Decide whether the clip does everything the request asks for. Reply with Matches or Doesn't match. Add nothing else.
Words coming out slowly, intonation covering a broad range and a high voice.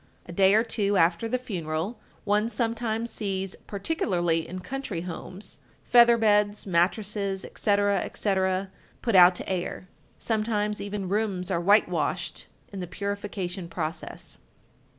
Doesn't match